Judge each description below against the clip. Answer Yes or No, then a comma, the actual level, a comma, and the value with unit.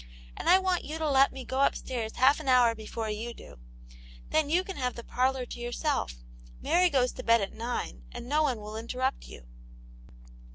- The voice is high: Yes, very high, 255 Hz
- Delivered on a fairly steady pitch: No, average, 4.0 semitones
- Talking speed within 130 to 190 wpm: No, average, 200 wpm